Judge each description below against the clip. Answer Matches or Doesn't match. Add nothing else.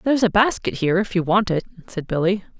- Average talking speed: Doesn't match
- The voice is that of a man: Doesn't match